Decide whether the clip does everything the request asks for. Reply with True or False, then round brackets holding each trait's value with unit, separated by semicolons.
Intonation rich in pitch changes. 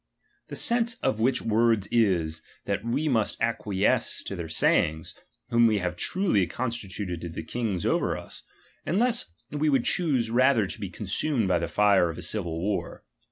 True (5.9 semitones)